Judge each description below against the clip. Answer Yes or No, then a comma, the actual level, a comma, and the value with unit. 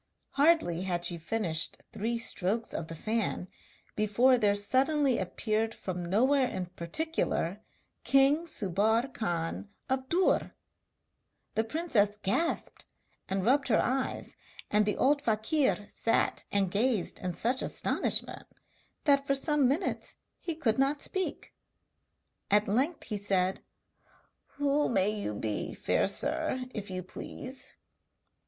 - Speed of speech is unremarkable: No, slow, 125 wpm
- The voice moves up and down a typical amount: No, wide, 6.0 semitones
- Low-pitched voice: No, high, 225 Hz